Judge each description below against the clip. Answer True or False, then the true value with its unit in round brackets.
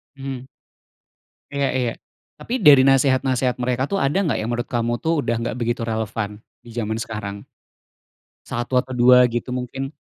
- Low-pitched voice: True (125 Hz)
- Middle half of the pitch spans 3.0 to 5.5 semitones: False (2.4 semitones)